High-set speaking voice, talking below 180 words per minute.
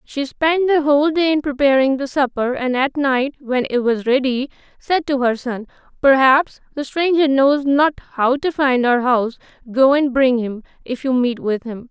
No: very high, 265 Hz; average, 195 wpm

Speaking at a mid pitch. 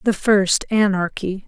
No: high, 195 Hz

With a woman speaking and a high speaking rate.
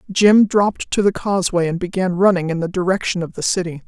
Yes: female; fast, 215 wpm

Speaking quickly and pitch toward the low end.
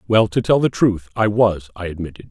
Yes: fast, 235 wpm; low, 100 Hz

